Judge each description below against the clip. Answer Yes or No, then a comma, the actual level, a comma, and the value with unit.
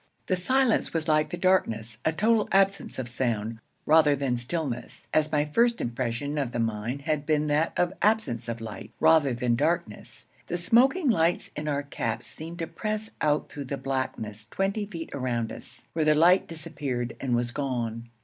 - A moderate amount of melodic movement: No, wide, 6.2 semitones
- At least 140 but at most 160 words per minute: No, average, 190 wpm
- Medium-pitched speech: Yes, medium, 150 Hz